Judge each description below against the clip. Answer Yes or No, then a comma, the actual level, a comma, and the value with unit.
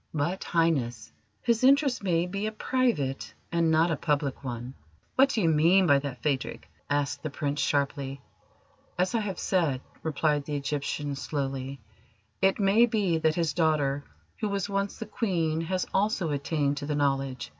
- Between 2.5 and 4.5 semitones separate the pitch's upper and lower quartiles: No, average, 5.3 semitones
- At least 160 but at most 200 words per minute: Yes, average, 165 wpm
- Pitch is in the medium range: Yes, medium, 160 Hz